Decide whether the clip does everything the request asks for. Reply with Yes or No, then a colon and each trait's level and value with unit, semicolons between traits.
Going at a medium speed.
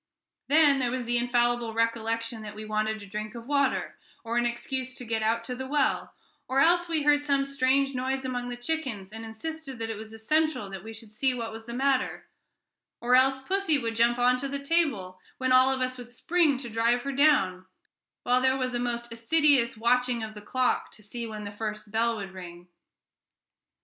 No: fast, 210 wpm